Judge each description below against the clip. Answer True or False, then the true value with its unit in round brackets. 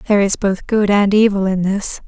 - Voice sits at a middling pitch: False (200 Hz)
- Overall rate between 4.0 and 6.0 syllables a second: True (5.4 syllables/s)